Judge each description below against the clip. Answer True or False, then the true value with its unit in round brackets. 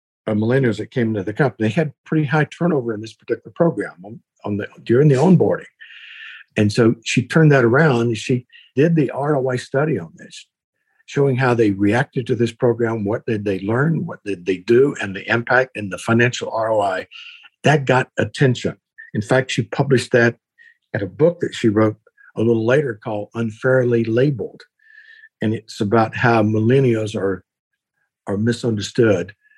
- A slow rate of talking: False (170 wpm)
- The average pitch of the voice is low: True (120 Hz)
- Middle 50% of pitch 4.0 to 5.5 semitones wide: True (4.5 semitones)